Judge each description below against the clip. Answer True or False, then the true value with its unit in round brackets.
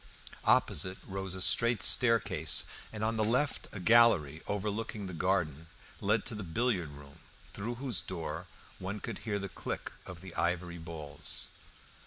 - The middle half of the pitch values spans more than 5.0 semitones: False (4.7 semitones)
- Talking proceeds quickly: False (155 wpm)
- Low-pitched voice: True (95 Hz)